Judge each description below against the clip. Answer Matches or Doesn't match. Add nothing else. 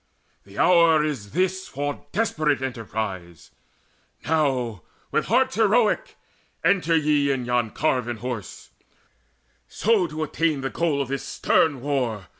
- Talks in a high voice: Doesn't match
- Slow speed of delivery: Matches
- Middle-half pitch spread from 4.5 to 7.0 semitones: Matches